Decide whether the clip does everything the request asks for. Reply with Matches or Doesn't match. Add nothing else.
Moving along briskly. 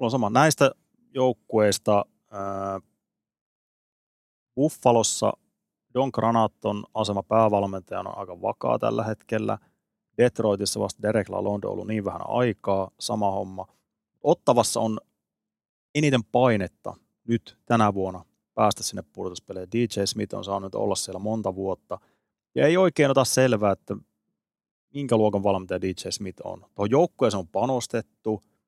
Doesn't match